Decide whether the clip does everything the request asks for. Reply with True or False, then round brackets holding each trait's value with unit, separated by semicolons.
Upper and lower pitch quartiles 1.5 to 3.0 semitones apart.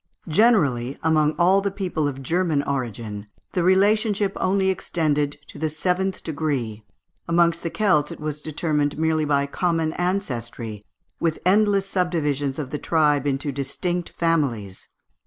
False (4.3 semitones)